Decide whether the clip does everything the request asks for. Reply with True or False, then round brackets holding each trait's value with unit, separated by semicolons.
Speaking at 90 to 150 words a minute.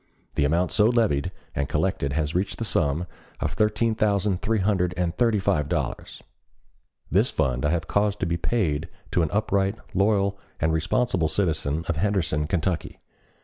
False (175 wpm)